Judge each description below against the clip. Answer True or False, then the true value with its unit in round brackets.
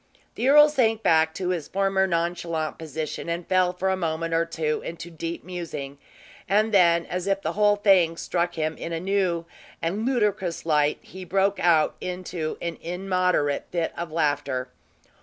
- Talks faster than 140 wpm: True (170 wpm)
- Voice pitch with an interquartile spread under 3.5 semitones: True (2.8 semitones)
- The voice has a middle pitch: True (175 Hz)